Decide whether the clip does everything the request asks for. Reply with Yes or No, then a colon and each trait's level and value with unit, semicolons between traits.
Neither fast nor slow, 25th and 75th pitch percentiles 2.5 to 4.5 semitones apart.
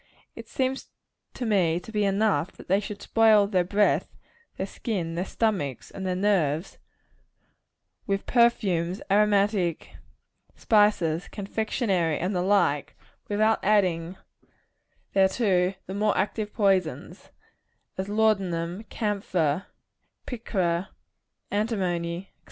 No: slow, 115 wpm; average, 3.1 semitones